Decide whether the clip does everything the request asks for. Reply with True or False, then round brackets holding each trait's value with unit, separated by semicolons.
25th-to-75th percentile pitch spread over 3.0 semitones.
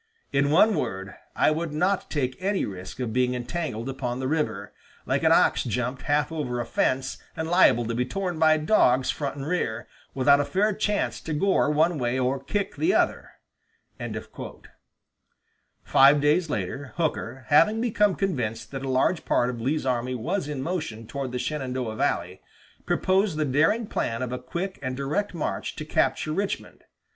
True (5.2 semitones)